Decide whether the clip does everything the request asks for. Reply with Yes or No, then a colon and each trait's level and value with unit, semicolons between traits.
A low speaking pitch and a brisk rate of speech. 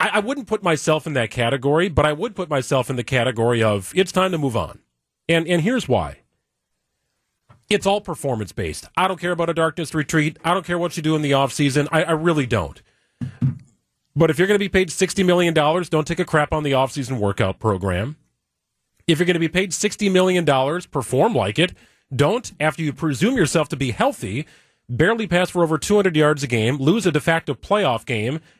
No: medium, 155 Hz; fast, 210 wpm